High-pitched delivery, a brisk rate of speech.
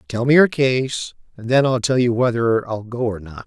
No: low, 120 Hz; fast, 245 wpm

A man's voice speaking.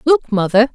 No: female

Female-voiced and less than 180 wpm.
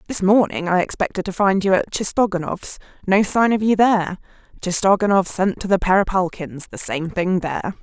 Yes: female; average, 160 wpm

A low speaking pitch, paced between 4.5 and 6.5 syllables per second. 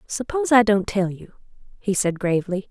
No: high, 205 Hz; 5.7 syllables/s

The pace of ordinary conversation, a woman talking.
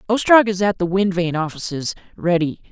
No: average, 175 wpm; male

